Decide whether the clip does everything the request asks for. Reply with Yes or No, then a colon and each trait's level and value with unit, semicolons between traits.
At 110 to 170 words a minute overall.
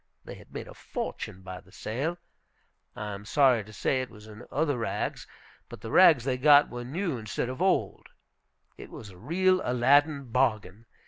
No: average, 185 wpm